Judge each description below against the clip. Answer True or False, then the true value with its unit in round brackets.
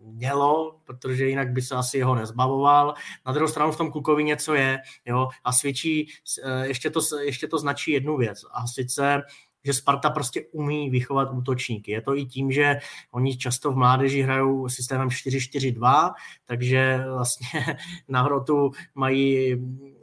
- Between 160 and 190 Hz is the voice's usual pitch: False (135 Hz)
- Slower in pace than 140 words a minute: False (155 wpm)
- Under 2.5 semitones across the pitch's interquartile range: True (2.1 semitones)